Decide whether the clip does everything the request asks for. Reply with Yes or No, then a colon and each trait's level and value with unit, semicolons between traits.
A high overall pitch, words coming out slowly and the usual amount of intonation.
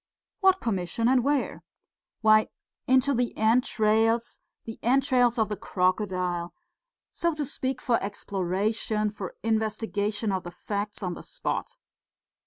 Yes: high, 220 Hz; slow, 125 wpm; average, 3.5 semitones